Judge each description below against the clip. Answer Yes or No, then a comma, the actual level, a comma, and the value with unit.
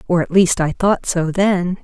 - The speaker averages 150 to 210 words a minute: No, fast, 230 wpm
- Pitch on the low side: No, medium, 180 Hz